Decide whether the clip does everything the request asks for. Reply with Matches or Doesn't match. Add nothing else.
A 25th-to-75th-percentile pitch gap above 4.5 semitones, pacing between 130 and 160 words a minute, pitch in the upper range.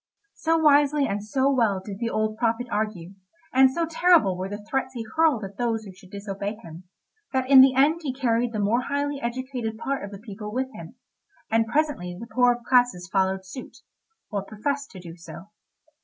Doesn't match